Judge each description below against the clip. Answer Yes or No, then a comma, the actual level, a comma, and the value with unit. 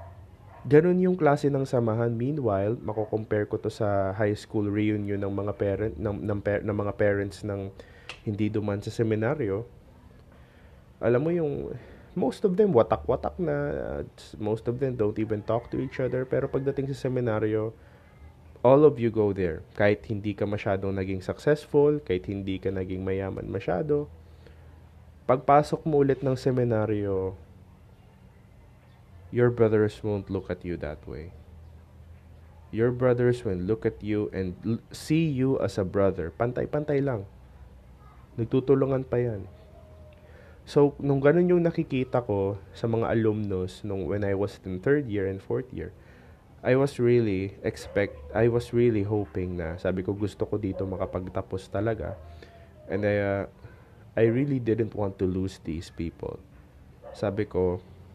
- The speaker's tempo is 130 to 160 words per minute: Yes, average, 150 wpm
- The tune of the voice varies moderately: Yes, average, 4.0 semitones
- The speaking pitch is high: No, low, 105 Hz